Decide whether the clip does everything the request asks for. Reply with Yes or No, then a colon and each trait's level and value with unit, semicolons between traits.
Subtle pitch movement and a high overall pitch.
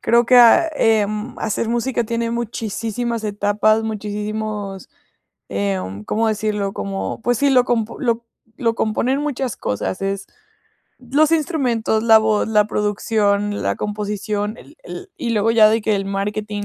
Yes: narrow, 2.3 semitones; high, 215 Hz